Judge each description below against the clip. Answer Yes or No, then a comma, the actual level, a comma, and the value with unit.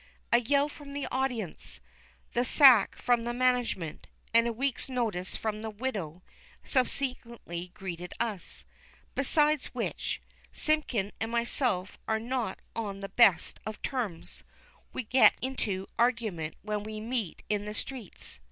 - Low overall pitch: No, high, 230 Hz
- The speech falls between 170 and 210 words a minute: No, slow, 135 wpm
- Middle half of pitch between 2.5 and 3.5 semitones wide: No, average, 4.2 semitones